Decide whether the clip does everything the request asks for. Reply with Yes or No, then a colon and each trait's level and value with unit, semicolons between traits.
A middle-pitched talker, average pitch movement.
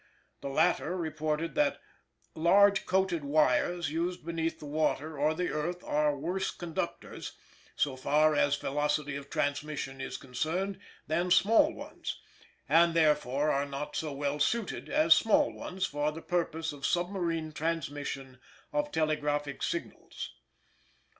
Yes: medium, 155 Hz; average, 3.2 semitones